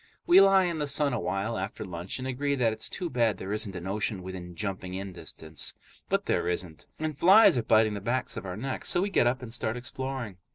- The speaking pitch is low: Yes, low, 110 Hz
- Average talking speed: No, fast, 235 wpm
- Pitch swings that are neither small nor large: No, wide, 6.2 semitones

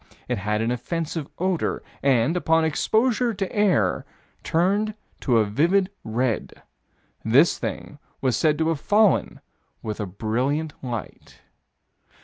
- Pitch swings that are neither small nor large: No, wide, 8.1 semitones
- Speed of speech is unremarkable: No, slow, 130 wpm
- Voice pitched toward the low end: No, medium, 150 Hz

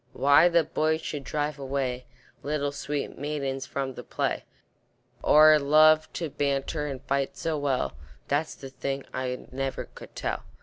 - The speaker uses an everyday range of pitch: No, narrow, 2.0 semitones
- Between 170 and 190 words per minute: No, average, 150 wpm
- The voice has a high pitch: No, medium, 140 Hz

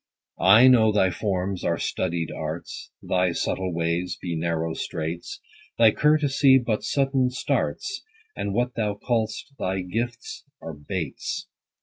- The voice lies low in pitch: Yes, low, 100 Hz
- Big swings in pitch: Yes, wide, 6.0 semitones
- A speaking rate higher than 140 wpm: No, slow, 135 wpm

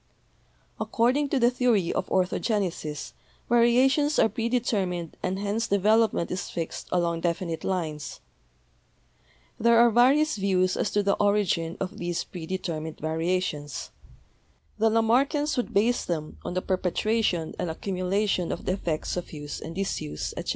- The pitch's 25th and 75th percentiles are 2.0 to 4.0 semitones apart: No, average, 5.1 semitones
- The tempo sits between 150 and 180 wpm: No, average, 140 wpm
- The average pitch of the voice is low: No, high, 190 Hz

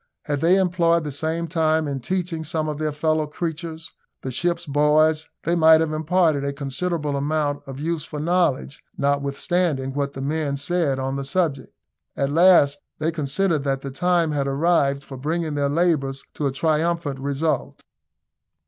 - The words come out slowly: No, average, 165 wpm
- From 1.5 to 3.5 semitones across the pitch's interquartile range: Yes, average, 3.0 semitones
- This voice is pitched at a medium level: Yes, medium, 155 Hz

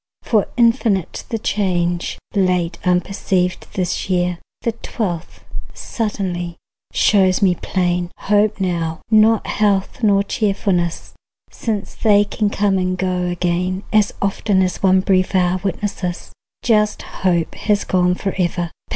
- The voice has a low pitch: No, high, 190 Hz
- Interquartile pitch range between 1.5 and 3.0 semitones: Yes, narrow, 2.5 semitones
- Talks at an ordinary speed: No, slow, 120 wpm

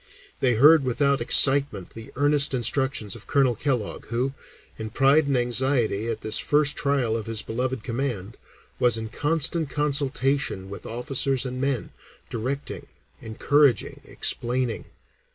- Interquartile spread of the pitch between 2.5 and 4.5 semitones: Yes, average, 3.6 semitones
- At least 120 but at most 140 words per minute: Yes, slow, 135 wpm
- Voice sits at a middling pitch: No, low, 130 Hz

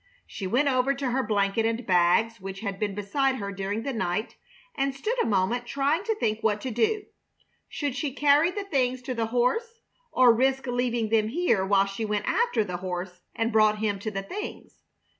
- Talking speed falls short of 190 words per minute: No, average, 200 wpm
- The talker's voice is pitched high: Yes, high, 230 Hz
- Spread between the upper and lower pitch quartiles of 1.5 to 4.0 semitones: No, average, 5.1 semitones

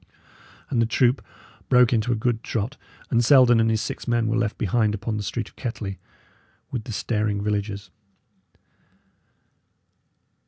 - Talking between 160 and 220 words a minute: No, average, 150 wpm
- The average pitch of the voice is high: No, low, 115 Hz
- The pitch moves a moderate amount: No, narrow, 2.3 semitones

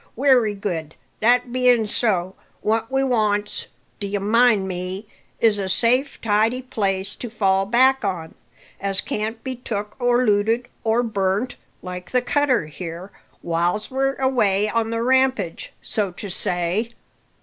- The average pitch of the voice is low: No, high, 215 Hz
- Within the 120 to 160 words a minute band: Yes, average, 140 wpm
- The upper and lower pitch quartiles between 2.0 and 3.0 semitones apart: No, average, 4.0 semitones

